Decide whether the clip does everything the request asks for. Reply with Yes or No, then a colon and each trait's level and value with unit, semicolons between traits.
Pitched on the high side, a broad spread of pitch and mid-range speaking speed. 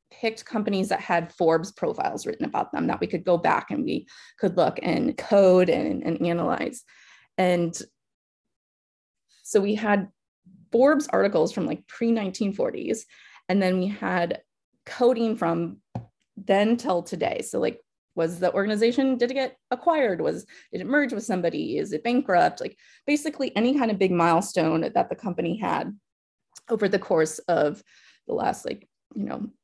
Yes: high, 200 Hz; wide, 5.7 semitones; average, 160 wpm